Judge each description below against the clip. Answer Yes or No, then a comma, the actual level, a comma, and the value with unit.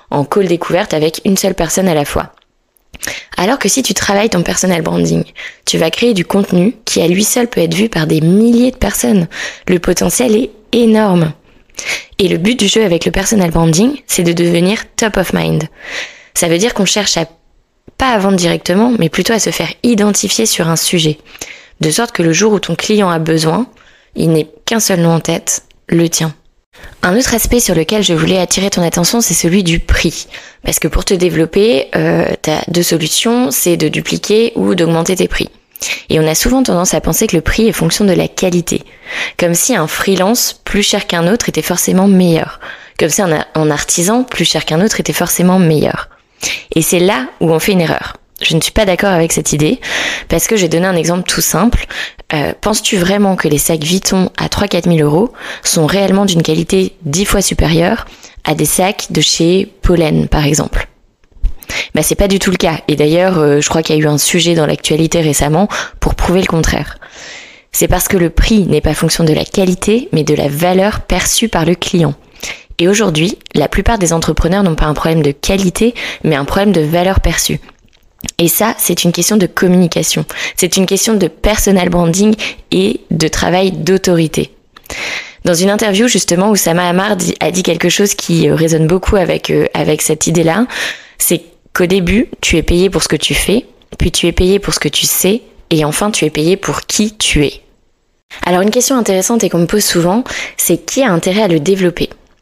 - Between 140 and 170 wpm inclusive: No, average, 205 wpm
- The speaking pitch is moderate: Yes, medium, 180 Hz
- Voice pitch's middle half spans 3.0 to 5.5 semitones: Yes, average, 3.8 semitones